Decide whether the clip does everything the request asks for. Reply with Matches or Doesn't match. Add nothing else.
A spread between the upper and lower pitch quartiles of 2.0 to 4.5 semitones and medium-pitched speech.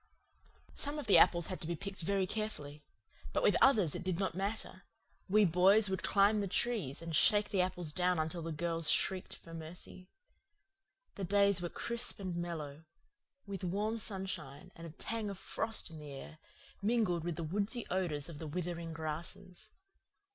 Matches